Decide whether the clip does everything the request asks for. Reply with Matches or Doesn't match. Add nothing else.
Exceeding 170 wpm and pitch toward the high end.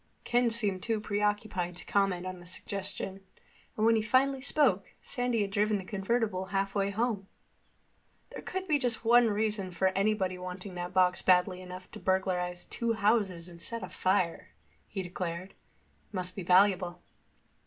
Doesn't match